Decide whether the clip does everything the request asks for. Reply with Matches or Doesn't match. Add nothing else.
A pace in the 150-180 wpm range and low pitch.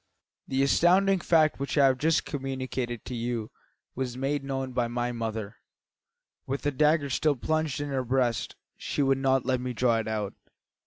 Matches